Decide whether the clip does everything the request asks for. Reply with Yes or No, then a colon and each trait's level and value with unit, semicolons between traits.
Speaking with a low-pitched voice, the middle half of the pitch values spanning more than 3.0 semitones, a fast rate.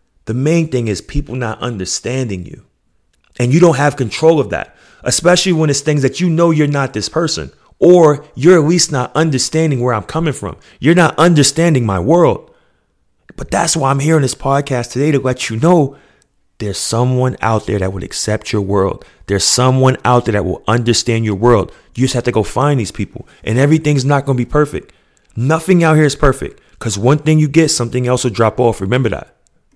Yes: low, 130 Hz; average, 5.1 semitones; fast, 210 wpm